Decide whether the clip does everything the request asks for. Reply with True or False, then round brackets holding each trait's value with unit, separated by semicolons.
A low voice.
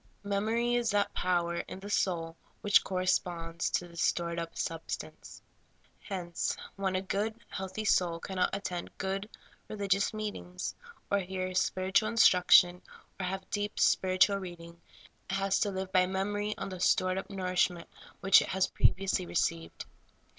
False (190 Hz)